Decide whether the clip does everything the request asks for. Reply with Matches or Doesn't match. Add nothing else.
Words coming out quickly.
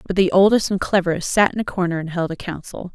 Matches